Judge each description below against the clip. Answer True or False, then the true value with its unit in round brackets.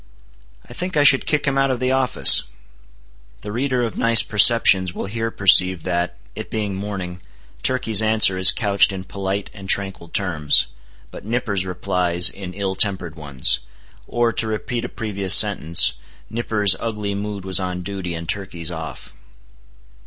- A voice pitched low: True (100 Hz)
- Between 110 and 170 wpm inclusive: True (160 wpm)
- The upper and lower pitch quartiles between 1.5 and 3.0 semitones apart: False (3.6 semitones)